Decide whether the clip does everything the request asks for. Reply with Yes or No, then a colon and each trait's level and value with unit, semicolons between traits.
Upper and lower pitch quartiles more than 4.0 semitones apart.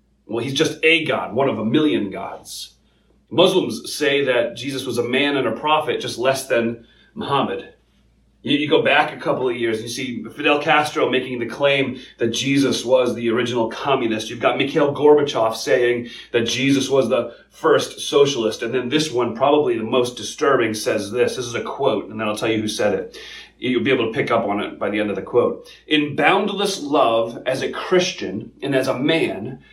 Yes: average, 4.4 semitones